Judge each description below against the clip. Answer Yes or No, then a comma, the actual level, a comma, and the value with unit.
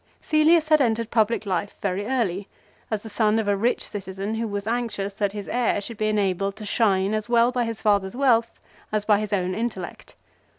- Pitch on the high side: Yes, high, 215 Hz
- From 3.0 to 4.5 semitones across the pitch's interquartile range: No, narrow, 2.6 semitones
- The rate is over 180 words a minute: Yes, fast, 205 wpm